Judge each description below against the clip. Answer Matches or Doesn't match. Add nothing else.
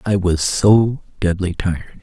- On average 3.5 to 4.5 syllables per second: Matches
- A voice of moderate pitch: Doesn't match